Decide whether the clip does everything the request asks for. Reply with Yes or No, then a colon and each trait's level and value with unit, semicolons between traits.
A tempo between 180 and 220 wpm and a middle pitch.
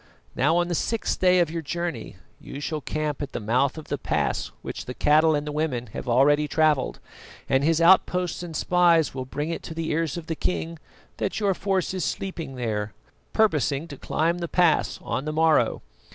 Yes: average, 200 wpm; medium, 160 Hz